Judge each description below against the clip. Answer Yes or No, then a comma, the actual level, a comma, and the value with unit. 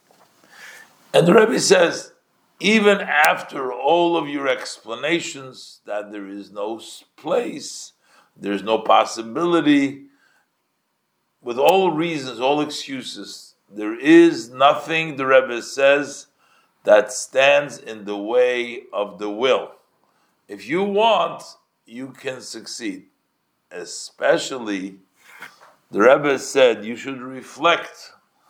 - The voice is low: No, medium, 145 Hz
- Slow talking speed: Yes, slow, 105 wpm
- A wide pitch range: Yes, wide, 6.4 semitones